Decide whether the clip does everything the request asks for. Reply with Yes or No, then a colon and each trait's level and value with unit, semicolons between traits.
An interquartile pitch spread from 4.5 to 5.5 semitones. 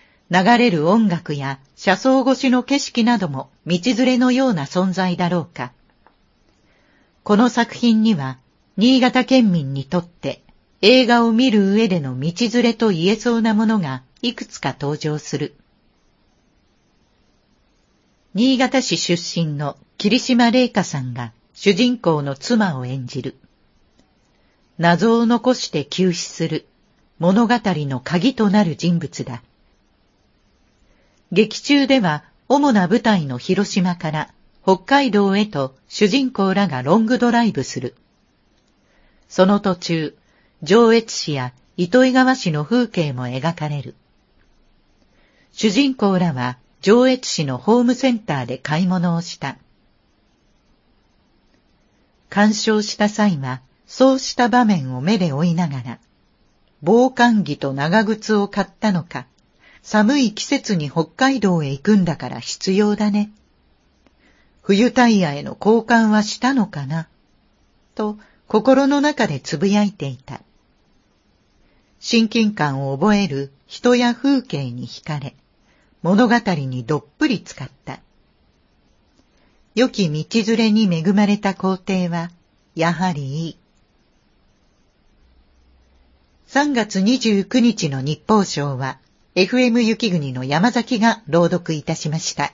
No: wide, 7.4 semitones